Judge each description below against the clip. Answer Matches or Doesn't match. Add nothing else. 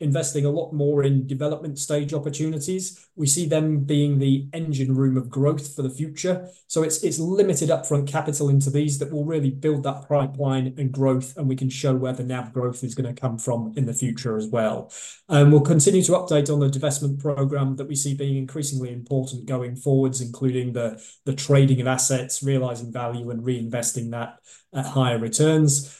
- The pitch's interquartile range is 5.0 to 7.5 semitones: Doesn't match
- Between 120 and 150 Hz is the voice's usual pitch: Matches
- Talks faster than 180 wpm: Matches